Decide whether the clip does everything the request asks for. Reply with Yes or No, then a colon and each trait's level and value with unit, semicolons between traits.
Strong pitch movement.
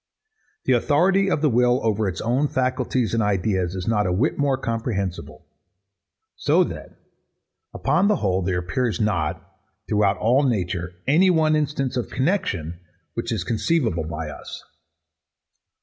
Yes: wide, 6.8 semitones